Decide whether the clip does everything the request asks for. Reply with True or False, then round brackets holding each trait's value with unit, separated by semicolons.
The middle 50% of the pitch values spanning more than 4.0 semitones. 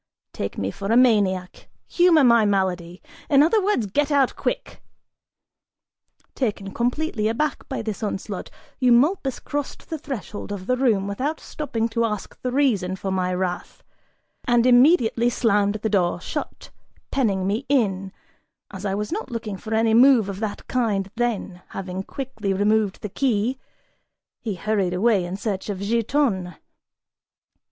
True (4.6 semitones)